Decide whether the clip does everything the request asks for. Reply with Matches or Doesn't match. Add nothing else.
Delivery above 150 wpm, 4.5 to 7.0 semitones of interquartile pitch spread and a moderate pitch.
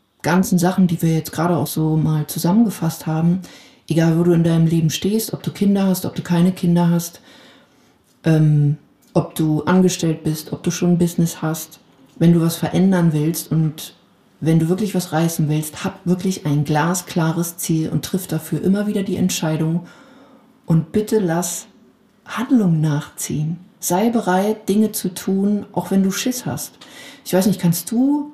Doesn't match